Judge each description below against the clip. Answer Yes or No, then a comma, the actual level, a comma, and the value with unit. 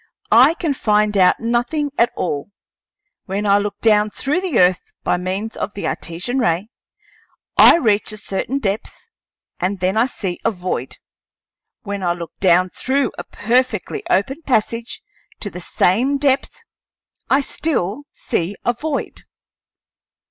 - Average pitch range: No, wide, 5.7 semitones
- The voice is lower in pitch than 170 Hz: No, high, 215 Hz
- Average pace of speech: Yes, average, 145 wpm